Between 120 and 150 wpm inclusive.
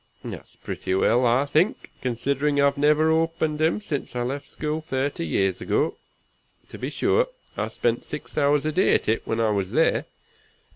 No: average, 180 wpm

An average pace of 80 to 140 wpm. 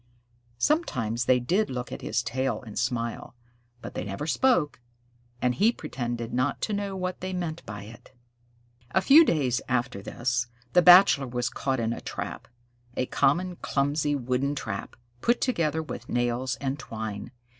No: average, 160 wpm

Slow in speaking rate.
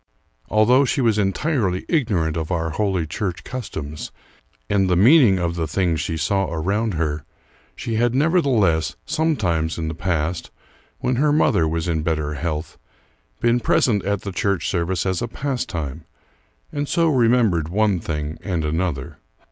No: average, 155 wpm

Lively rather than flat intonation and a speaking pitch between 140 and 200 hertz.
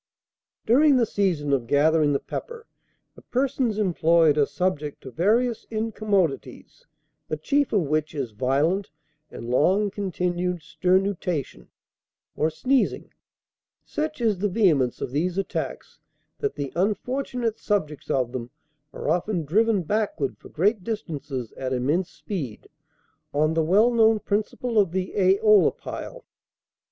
Yes: wide, 6.5 semitones; medium, 185 Hz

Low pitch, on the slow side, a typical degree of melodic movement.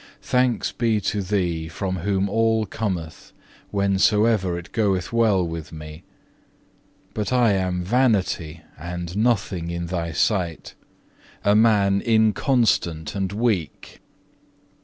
Yes: low, 100 Hz; slow, 115 wpm; average, 4.1 semitones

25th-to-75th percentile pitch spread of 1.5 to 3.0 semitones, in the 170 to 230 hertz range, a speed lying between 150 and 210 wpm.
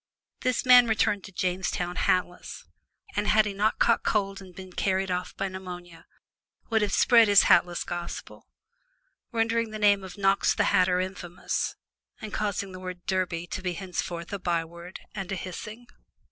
Yes: narrow, 2.5 semitones; high, 190 Hz; average, 165 wpm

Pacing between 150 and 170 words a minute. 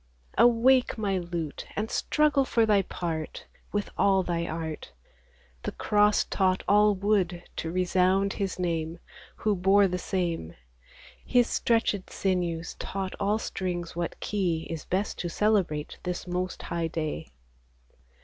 No: slow, 135 wpm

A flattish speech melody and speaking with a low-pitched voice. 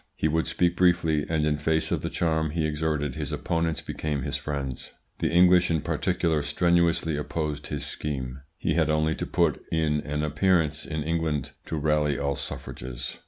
Yes: narrow, 2.0 semitones; very low, 75 Hz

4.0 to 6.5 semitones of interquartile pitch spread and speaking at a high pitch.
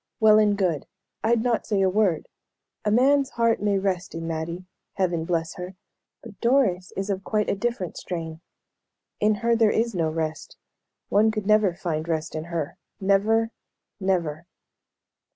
Yes: average, 4.4 semitones; high, 195 Hz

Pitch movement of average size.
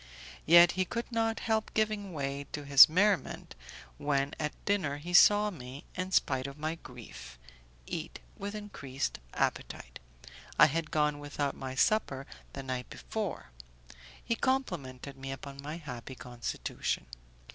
No: wide, 6.5 semitones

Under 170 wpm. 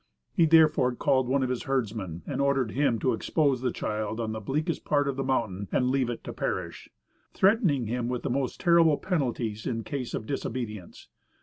No: average, 195 wpm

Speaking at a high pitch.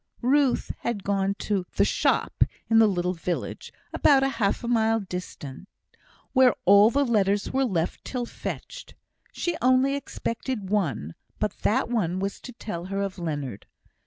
Yes: high, 205 Hz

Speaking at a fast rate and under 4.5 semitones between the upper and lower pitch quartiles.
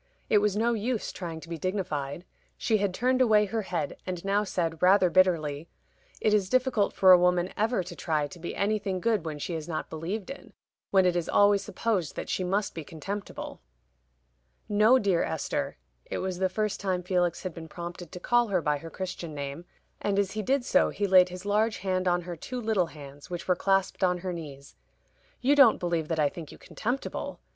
Yes: fast, 210 wpm; average, 3.6 semitones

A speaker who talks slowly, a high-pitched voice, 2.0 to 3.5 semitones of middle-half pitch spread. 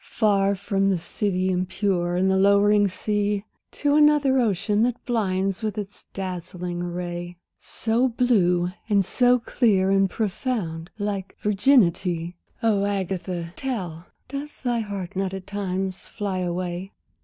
Yes: slow, 130 wpm; high, 195 Hz; average, 3.0 semitones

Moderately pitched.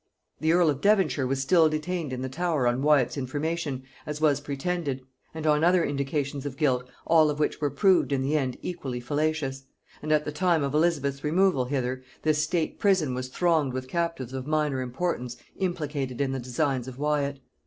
Yes: medium, 145 Hz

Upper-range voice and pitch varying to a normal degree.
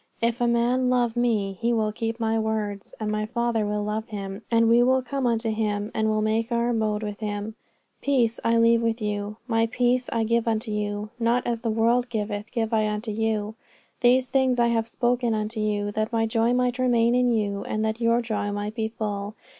No: high, 225 Hz; narrow, 1.9 semitones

